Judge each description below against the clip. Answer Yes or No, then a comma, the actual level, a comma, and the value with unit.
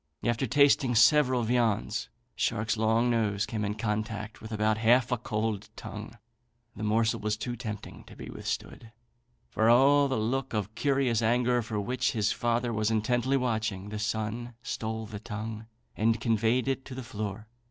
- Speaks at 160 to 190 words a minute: Yes, average, 165 wpm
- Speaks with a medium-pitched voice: No, low, 115 Hz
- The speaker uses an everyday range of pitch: No, narrow, 2.2 semitones